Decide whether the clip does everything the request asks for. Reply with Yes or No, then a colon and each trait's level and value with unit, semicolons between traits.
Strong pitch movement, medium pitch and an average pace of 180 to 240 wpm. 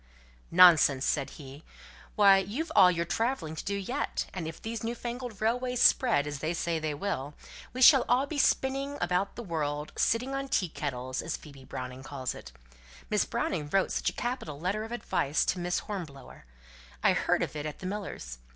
Yes: wide, 7.8 semitones; medium, 180 Hz; average, 190 wpm